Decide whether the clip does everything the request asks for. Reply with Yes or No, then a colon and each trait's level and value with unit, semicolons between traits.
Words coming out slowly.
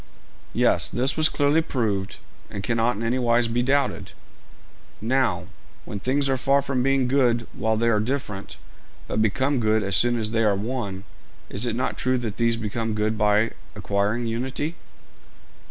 No: average, 170 wpm